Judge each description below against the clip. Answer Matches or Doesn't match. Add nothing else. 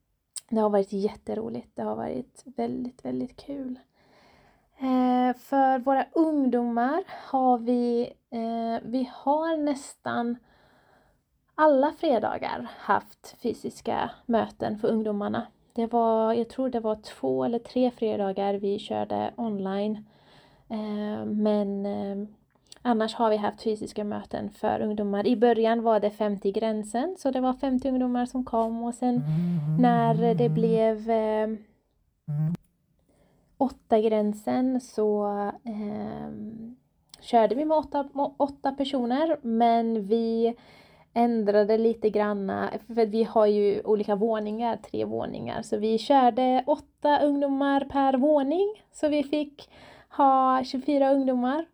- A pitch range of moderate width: Matches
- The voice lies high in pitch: Matches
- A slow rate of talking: Matches